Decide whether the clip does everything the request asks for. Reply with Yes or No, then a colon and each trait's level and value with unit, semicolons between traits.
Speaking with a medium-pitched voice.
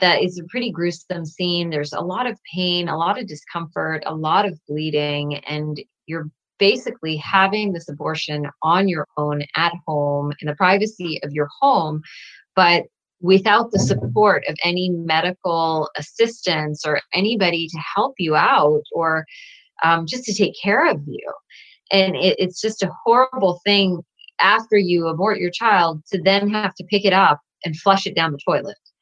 Yes: medium, 175 Hz